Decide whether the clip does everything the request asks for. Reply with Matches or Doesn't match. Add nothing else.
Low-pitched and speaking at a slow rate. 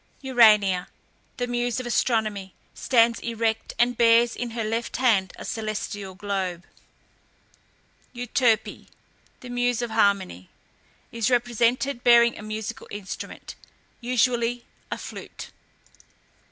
Doesn't match